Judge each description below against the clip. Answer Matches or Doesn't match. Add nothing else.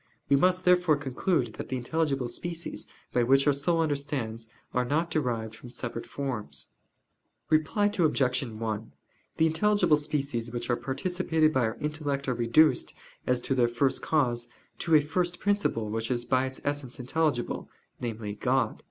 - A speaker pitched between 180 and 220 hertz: Doesn't match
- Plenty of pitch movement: Doesn't match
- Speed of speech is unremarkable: Matches